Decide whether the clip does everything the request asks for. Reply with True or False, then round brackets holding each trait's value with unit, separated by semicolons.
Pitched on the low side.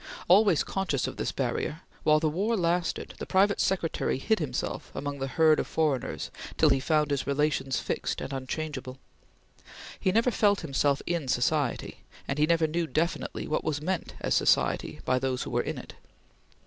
False (155 Hz)